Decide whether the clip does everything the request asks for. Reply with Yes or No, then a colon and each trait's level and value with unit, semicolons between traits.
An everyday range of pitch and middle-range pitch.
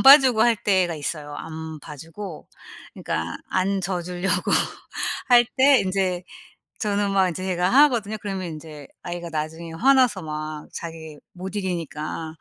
Yes: average, 4.1 semitones; medium, 180 Hz